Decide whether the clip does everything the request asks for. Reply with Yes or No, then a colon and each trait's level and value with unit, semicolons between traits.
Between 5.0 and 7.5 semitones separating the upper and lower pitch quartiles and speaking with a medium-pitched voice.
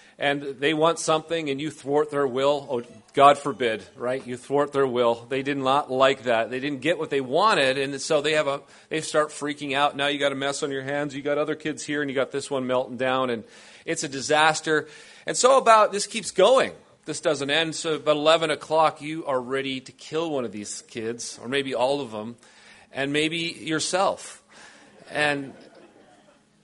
No: narrow, 2.4 semitones; medium, 145 Hz